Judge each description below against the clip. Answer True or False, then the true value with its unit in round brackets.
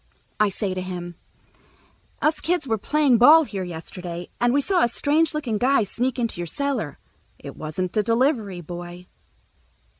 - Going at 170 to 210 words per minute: False (160 wpm)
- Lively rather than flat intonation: True (7.6 semitones)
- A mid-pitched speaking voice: False (220 Hz)